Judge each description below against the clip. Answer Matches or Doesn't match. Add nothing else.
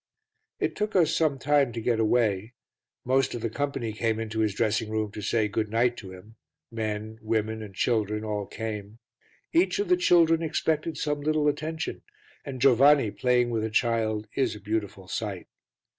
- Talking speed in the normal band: Matches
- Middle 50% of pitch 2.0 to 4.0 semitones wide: Doesn't match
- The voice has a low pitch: Matches